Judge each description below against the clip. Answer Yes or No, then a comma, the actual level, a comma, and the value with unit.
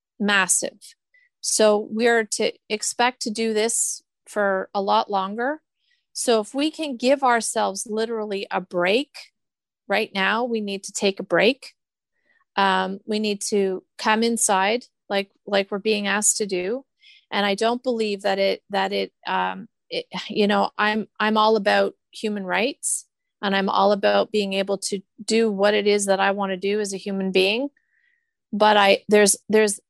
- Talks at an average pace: Yes, average, 170 wpm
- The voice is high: Yes, high, 210 Hz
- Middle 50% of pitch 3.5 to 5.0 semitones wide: No, average, 3.0 semitones